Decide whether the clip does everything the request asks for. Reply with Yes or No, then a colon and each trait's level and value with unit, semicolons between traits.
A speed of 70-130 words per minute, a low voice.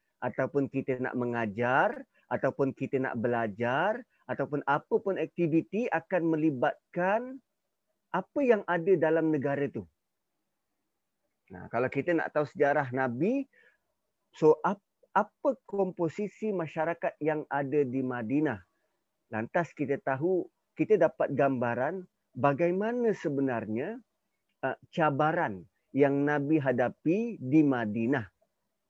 No: average, 105 wpm; medium, 150 Hz